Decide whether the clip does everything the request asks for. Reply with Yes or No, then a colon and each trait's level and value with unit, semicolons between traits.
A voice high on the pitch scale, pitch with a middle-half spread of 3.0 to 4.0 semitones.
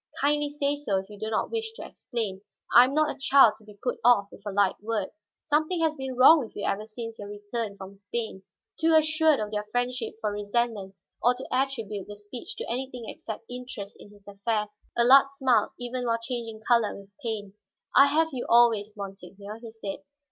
No: high, 230 Hz; average, 4.4 semitones